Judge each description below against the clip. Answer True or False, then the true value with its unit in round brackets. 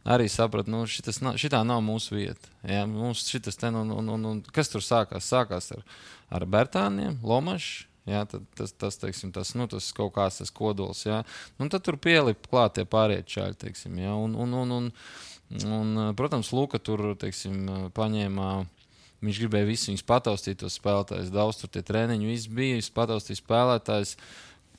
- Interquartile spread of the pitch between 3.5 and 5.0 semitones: False (2.9 semitones)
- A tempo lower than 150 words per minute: True (135 wpm)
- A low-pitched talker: True (110 Hz)